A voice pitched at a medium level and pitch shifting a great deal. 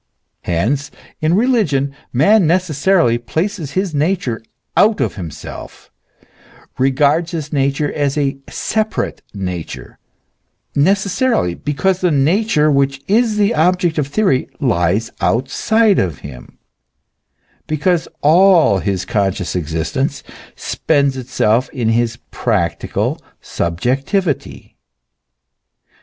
Yes: medium, 145 Hz; wide, 7.4 semitones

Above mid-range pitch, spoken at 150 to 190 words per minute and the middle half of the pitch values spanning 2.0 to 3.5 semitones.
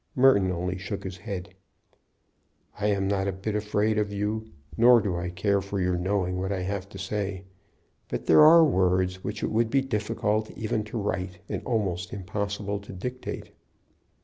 No: low, 100 Hz; average, 175 wpm; narrow, 2.5 semitones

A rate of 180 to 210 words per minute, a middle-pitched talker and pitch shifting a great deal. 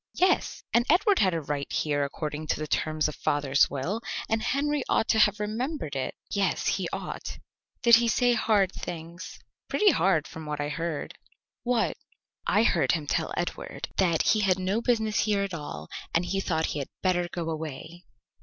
Yes: average, 185 wpm; medium, 180 Hz; wide, 6.2 semitones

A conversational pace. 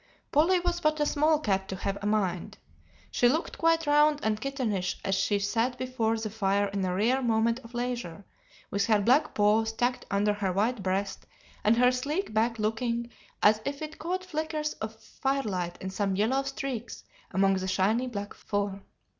Yes: average, 180 wpm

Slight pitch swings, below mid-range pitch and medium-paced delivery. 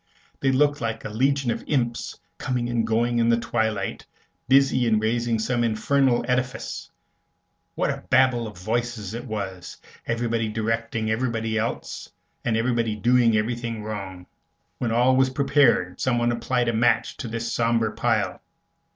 Yes: narrow, 1.9 semitones; low, 115 Hz; average, 150 wpm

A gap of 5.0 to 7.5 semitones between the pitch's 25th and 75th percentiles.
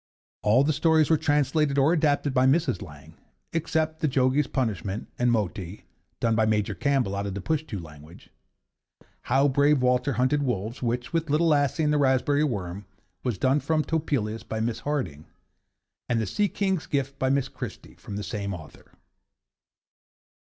Yes: wide, 5.6 semitones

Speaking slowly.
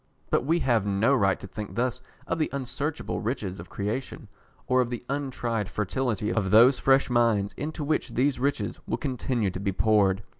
No: average, 185 wpm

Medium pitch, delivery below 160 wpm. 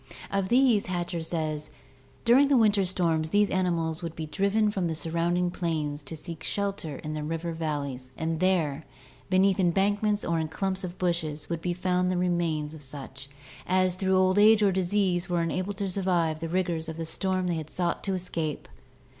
No: medium, 175 Hz; average, 190 wpm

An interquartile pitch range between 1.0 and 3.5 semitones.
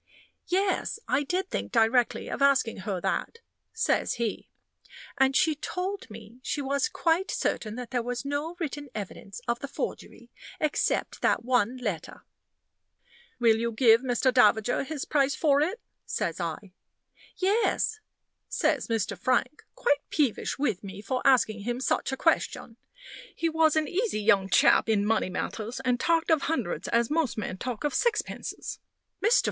No: wide, 5.5 semitones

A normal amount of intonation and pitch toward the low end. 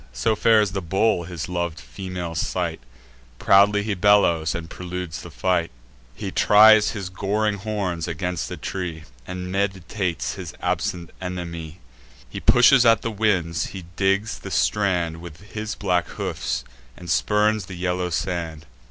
Yes: average, 3.4 semitones; very low, 90 Hz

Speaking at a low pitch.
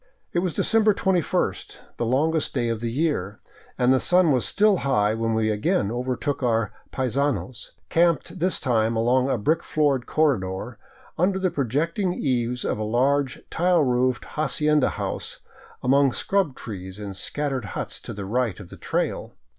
Yes: low, 130 Hz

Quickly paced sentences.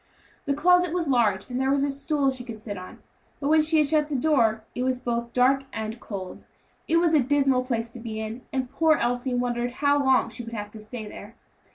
Yes: fast, 235 wpm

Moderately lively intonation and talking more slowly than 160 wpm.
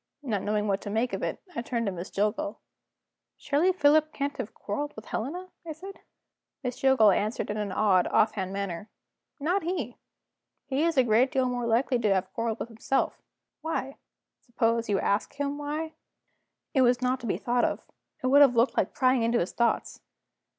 No: average, 5.0 semitones; average, 190 wpm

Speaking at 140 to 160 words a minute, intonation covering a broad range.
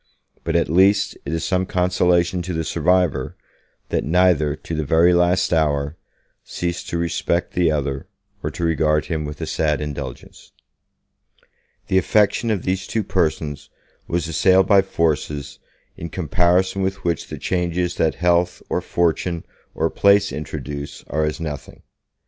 No: average, 150 wpm; average, 2.9 semitones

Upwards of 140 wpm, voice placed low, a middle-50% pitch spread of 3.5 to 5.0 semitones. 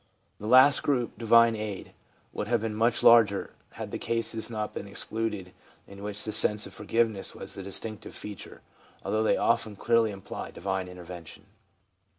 No: average, 165 wpm; low, 110 Hz; narrow, 2.6 semitones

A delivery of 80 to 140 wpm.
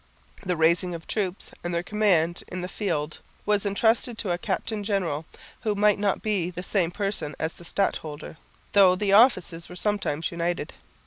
No: average, 175 wpm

